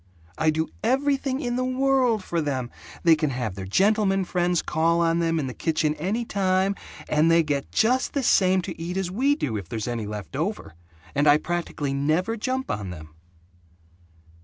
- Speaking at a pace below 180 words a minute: No, average, 185 wpm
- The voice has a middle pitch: Yes, medium, 170 Hz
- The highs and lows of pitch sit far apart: Yes, wide, 6.8 semitones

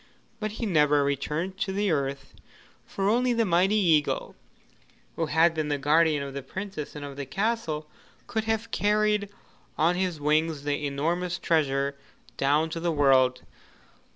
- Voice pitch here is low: No, medium, 160 Hz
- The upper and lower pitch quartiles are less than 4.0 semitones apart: No, average, 5.2 semitones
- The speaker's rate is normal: Yes, average, 155 wpm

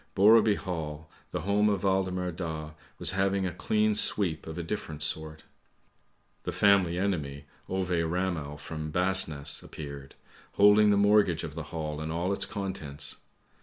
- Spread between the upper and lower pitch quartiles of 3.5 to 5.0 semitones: Yes, average, 4.0 semitones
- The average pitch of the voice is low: Yes, very low, 90 Hz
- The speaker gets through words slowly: No, average, 150 wpm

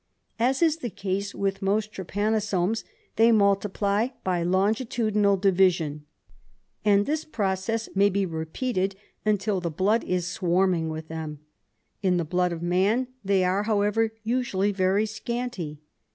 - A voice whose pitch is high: Yes, high, 195 Hz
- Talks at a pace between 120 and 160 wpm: Yes, average, 140 wpm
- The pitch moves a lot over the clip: No, average, 3.2 semitones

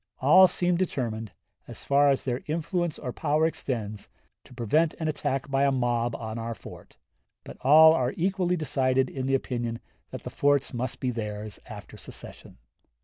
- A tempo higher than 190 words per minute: No, average, 170 wpm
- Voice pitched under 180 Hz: Yes, low, 135 Hz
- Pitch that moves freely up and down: No, average, 4.7 semitones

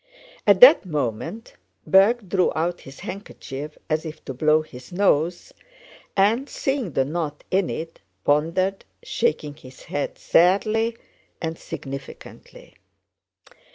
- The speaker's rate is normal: No, slow, 120 wpm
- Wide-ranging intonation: No, average, 5.0 semitones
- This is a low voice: No, medium, 165 Hz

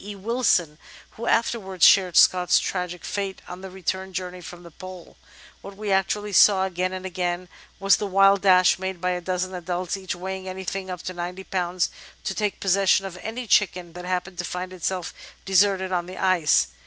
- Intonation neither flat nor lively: No, narrow, 1.4 semitones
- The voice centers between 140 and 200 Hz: Yes, medium, 185 Hz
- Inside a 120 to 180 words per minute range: No, average, 190 wpm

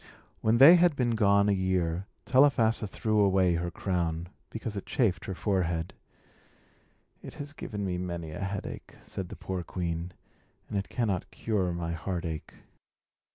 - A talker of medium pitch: No, very low, 95 Hz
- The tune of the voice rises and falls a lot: No, average, 3.8 semitones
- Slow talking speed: No, average, 155 wpm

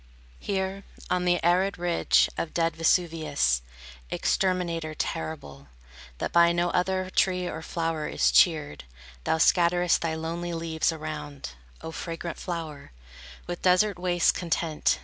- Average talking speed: No, slow, 130 wpm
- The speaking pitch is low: No, medium, 170 Hz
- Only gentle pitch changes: Yes, narrow, 2.0 semitones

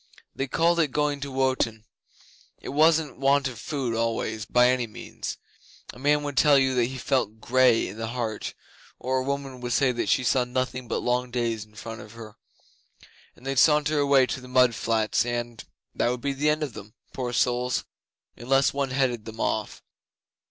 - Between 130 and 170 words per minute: No, average, 195 wpm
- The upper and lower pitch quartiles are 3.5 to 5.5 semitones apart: No, average, 2.8 semitones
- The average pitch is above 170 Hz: No, low, 125 Hz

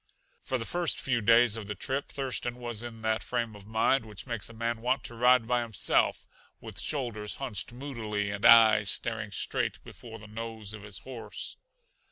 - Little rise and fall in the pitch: Yes, narrow, 2.3 semitones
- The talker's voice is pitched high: No, low, 115 Hz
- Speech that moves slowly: No, average, 190 wpm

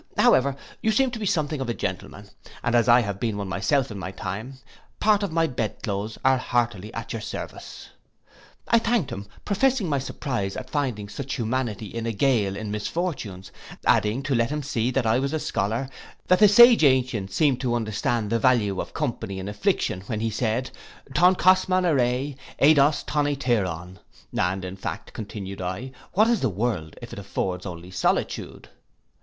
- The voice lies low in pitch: Yes, low, 120 Hz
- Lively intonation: Yes, wide, 5.9 semitones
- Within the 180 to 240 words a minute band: Yes, average, 185 wpm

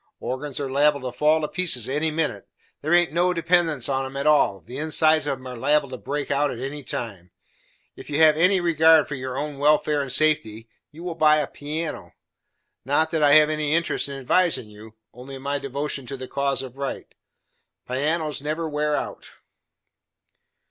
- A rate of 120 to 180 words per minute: No, average, 190 wpm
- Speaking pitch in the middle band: Yes, medium, 145 Hz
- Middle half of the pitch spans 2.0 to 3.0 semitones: Yes, average, 2.7 semitones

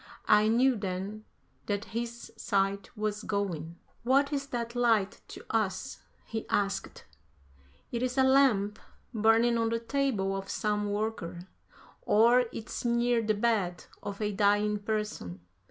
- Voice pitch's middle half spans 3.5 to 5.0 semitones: No, average, 2.7 semitones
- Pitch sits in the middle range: No, high, 215 Hz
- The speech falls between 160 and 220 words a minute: No, average, 140 wpm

